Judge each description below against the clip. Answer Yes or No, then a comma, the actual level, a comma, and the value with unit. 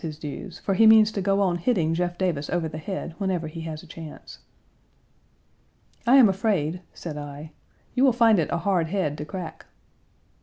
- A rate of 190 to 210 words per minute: Yes, average, 200 wpm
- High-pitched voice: No, medium, 175 Hz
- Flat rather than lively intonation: No, average, 4.0 semitones